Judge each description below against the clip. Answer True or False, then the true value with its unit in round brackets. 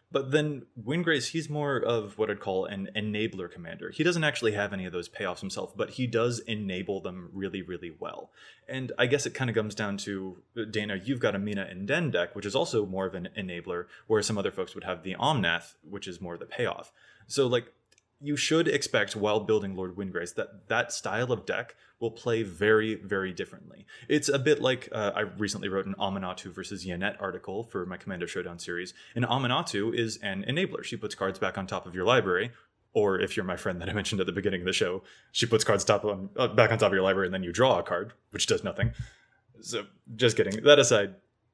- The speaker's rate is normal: False (225 wpm)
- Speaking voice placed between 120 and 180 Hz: False (105 Hz)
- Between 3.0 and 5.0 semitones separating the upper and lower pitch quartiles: True (3.8 semitones)